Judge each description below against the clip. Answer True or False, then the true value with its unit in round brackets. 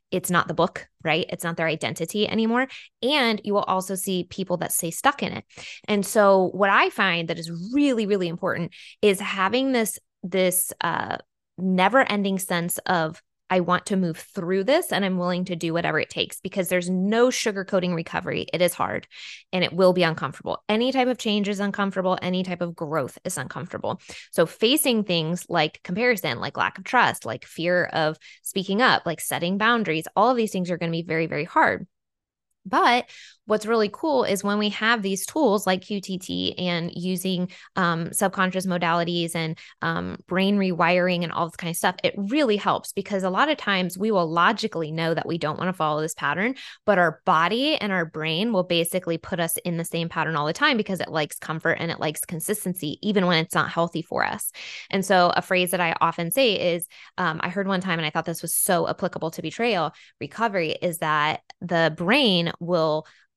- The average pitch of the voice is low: False (180 Hz)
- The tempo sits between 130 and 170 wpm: False (205 wpm)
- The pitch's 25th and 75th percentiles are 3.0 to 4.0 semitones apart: True (3.5 semitones)